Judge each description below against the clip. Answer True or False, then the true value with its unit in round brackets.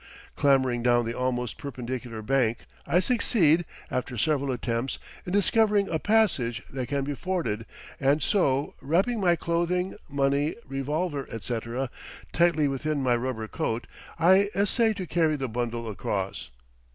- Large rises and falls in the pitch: True (6.0 semitones)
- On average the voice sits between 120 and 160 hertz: True (140 Hz)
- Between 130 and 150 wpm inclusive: True (140 wpm)